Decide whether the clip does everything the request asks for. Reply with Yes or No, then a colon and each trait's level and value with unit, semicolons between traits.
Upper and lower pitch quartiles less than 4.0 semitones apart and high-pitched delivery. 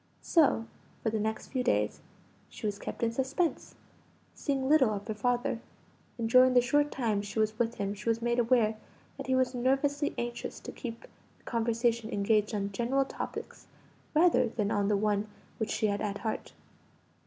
Yes: average, 3.3 semitones; high, 230 Hz